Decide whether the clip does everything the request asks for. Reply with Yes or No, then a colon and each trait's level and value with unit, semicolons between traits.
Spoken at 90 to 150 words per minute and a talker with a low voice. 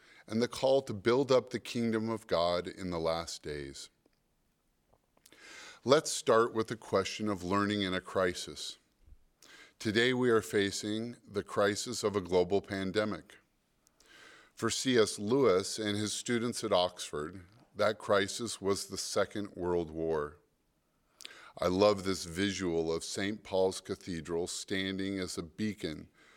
Yes: average, 140 wpm; low, 100 Hz